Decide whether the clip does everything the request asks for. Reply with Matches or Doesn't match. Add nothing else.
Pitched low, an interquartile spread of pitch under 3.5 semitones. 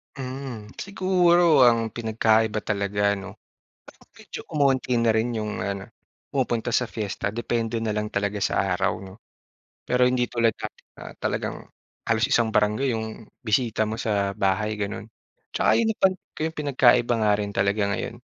Matches